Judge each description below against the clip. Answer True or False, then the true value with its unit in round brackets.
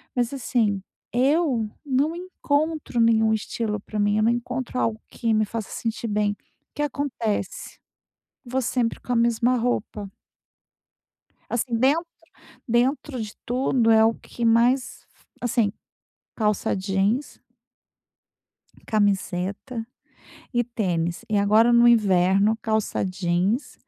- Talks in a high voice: True (230 Hz)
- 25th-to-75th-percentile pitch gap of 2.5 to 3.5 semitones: True (3.0 semitones)